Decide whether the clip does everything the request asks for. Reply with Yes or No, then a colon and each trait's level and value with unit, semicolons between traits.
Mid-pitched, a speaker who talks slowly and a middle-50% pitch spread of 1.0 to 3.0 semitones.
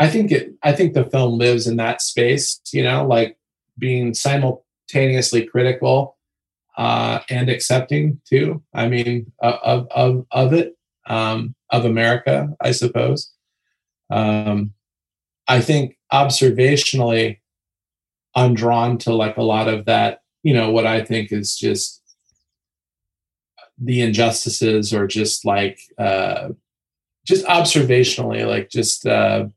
No: low, 120 Hz; slow, 130 wpm; average, 2.7 semitones